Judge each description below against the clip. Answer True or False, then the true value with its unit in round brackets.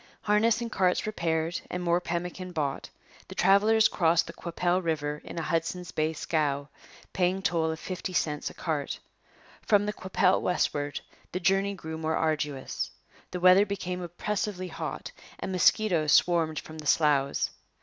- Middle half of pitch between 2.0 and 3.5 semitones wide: True (2.9 semitones)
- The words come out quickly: False (155 wpm)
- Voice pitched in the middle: True (175 Hz)